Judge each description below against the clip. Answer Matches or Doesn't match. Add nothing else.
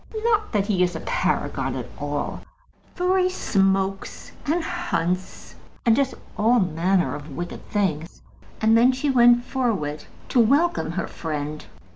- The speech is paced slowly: Doesn't match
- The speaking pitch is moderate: Doesn't match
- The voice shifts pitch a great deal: Matches